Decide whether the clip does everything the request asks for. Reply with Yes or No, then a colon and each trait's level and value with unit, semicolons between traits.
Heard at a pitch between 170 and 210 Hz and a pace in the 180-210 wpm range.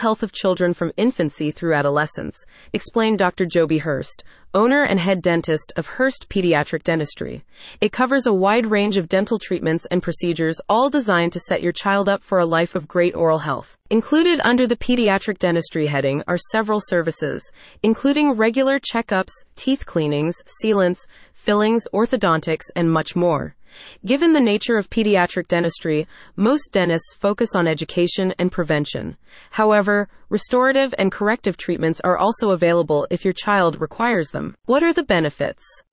No: high, 190 Hz; average, 155 wpm